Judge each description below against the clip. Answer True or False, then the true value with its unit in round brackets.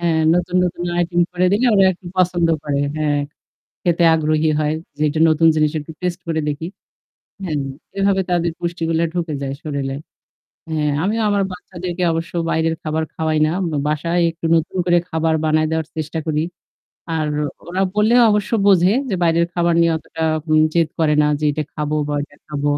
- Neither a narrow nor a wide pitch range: False (2.3 semitones)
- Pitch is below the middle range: False (165 Hz)